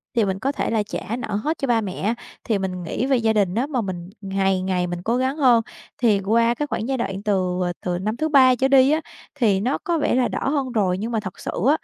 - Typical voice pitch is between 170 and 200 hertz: No, high, 225 Hz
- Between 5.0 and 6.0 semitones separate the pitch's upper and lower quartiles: Yes, average, 5.3 semitones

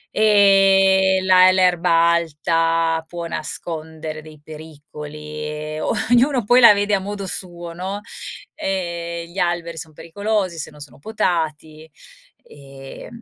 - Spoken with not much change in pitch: No, average, 3.5 semitones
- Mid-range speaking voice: Yes, medium, 170 Hz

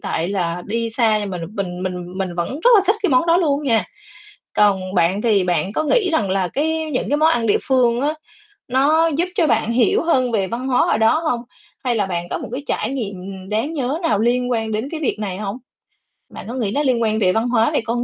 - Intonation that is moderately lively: No, wide, 6.0 semitones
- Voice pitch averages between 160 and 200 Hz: No, high, 230 Hz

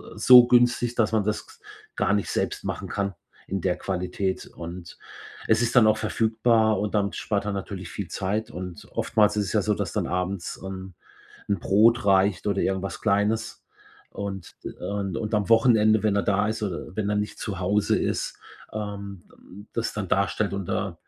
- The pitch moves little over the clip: Yes, narrow, 2.1 semitones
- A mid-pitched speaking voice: No, low, 100 Hz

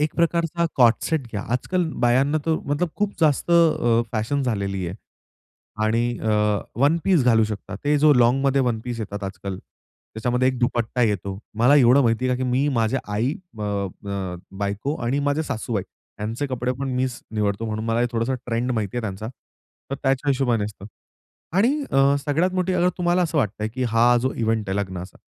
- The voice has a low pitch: Yes, low, 120 Hz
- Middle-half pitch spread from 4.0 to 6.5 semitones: Yes, average, 4.7 semitones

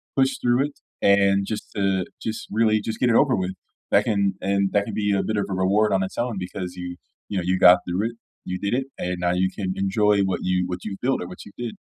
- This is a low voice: Yes, low, 100 Hz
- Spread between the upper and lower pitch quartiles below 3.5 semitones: Yes, average, 2.7 semitones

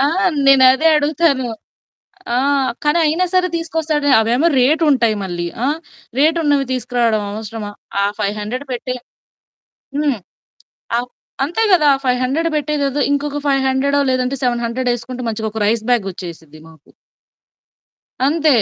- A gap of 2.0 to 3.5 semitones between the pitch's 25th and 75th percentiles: No, average, 4.3 semitones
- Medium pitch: No, very high, 260 Hz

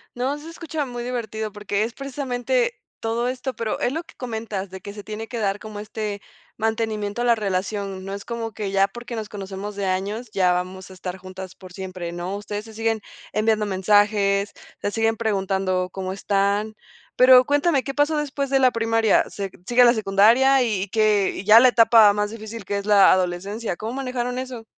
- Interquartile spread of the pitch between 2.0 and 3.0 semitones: No, average, 3.4 semitones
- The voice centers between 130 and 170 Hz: No, high, 215 Hz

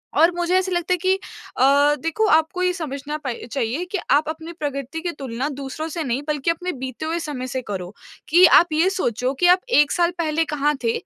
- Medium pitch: No, very high, 310 Hz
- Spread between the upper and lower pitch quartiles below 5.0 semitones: Yes, average, 4.1 semitones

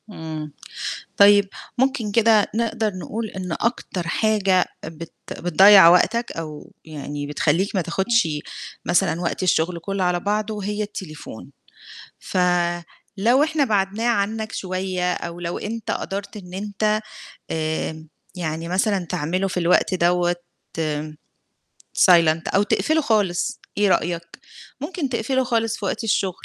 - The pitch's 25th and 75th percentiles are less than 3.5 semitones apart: No, average, 4.1 semitones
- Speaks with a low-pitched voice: No, high, 190 Hz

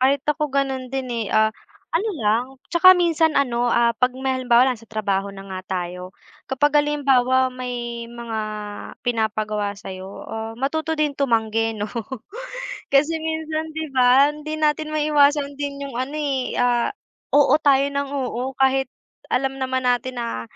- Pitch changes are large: No, average, 3.7 semitones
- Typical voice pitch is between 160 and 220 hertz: No, very high, 260 Hz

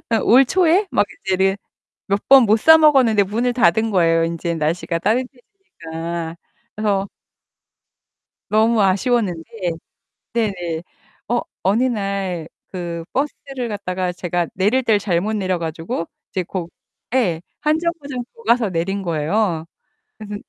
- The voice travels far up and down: Yes, wide, 5.7 semitones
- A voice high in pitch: Yes, high, 200 Hz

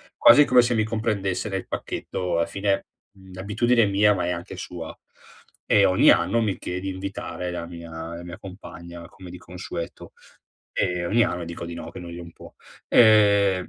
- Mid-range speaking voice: No, very low, 95 Hz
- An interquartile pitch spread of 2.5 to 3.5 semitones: Yes, average, 2.9 semitones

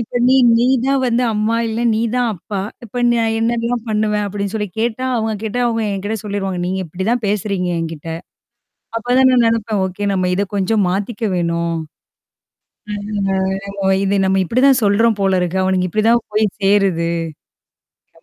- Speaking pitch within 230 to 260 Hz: No, high, 210 Hz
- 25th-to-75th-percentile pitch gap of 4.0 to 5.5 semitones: No, average, 3.2 semitones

